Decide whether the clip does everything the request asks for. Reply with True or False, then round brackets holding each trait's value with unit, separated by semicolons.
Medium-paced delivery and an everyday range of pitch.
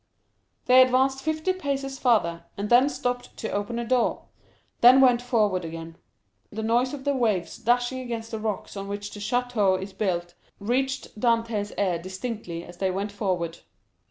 True (165 wpm; 4.3 semitones)